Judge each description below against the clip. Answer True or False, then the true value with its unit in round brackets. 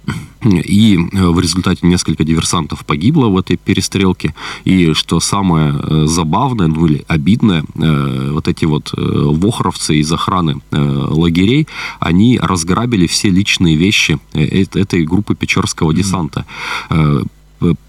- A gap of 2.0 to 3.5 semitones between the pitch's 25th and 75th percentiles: True (3.2 semitones)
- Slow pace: True (105 wpm)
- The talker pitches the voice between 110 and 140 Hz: False (85 Hz)